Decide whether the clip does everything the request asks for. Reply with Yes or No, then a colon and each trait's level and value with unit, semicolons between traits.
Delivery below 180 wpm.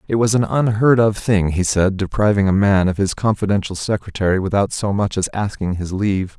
No: fast, 205 wpm